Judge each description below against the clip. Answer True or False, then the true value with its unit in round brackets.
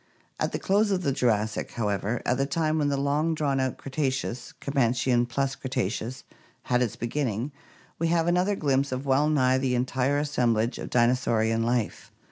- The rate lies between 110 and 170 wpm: False (180 wpm)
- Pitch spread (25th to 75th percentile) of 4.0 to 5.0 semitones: False (3.3 semitones)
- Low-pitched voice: True (130 Hz)